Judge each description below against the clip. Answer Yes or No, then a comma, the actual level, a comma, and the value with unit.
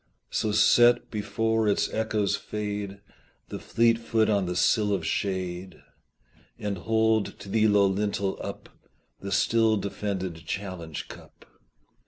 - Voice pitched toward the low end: Yes, low, 105 Hz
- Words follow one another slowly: Yes, slow, 130 wpm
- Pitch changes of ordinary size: No, narrow, 2.3 semitones